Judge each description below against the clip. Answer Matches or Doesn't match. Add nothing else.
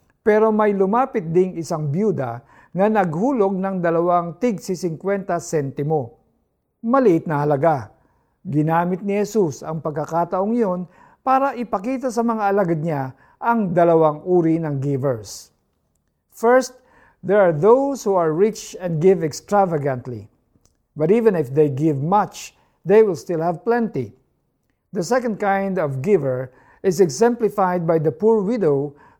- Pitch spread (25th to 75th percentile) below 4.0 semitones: Doesn't match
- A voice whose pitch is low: Doesn't match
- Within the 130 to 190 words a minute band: Matches